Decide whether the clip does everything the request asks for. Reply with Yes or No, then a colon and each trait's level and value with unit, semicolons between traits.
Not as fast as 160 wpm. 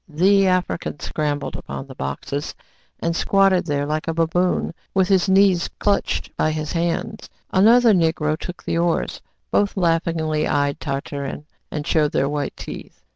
Yes: average, 150 wpm